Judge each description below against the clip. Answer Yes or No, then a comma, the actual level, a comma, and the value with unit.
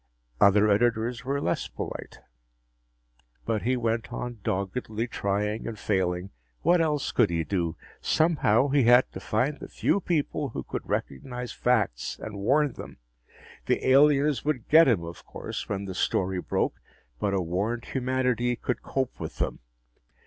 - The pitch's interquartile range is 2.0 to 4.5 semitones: No, average, 4.9 semitones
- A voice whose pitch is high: No, low, 115 Hz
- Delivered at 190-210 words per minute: No, average, 155 wpm